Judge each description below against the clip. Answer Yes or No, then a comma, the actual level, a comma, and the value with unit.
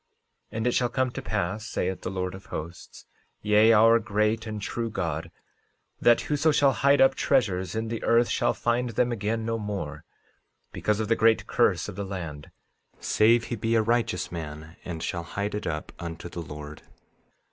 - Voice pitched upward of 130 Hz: No, low, 105 Hz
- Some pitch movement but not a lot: Yes, average, 4.6 semitones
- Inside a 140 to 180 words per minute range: No, average, 190 wpm